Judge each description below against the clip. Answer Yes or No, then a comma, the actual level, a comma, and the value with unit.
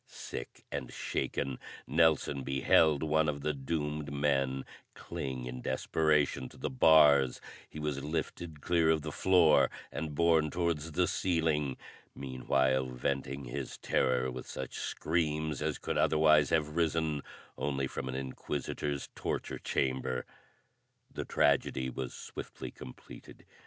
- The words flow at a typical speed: No, slow, 130 wpm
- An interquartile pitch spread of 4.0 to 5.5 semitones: No, average, 2.9 semitones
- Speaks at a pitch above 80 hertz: No, very low, 75 Hz